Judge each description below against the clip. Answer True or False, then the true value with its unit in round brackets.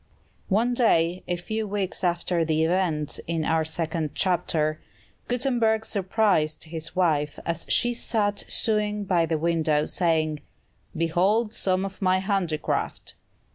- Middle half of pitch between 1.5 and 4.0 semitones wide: False (4.4 semitones)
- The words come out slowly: True (130 wpm)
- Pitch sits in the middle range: True (175 Hz)